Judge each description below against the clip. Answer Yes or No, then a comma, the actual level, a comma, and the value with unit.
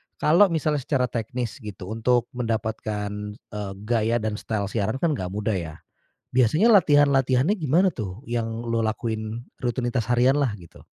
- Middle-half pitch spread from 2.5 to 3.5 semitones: No, average, 3.9 semitones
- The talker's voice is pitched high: No, low, 120 Hz